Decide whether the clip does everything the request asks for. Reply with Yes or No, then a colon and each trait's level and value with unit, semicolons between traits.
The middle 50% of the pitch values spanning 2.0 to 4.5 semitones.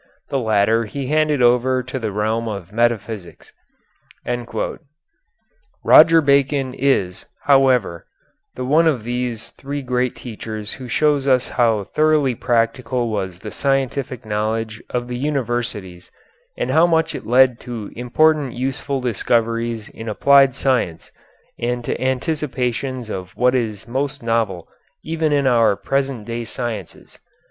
Yes: average, 3.4 semitones